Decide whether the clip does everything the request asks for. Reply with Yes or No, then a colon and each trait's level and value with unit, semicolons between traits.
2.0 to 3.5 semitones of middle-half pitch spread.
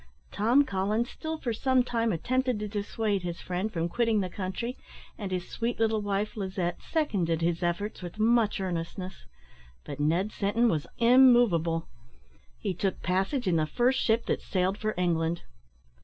No: average, 4.7 semitones